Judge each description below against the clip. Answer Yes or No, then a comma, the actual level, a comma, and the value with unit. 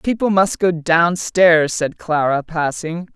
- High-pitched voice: No, medium, 170 Hz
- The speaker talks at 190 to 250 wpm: No, slow, 135 wpm